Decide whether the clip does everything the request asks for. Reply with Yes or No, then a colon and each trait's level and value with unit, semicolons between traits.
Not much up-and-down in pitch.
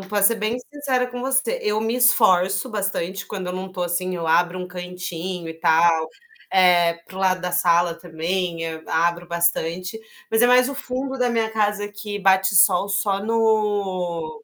No: average, 3.7 semitones